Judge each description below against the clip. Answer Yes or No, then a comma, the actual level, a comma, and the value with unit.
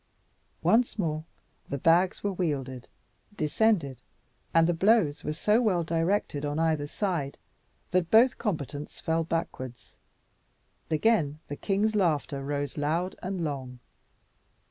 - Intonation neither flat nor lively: Yes, average, 4.7 semitones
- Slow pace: Yes, slow, 120 wpm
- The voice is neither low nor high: Yes, medium, 165 Hz